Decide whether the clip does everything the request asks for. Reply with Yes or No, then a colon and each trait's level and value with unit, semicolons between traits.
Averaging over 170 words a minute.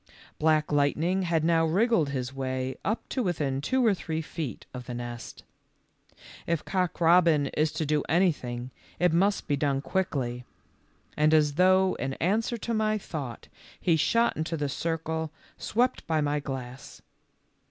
No: average, 155 wpm